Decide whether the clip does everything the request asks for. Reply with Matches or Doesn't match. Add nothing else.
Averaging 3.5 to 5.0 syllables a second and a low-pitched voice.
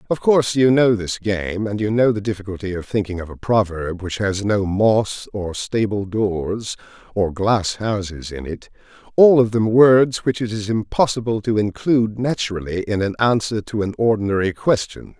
Matches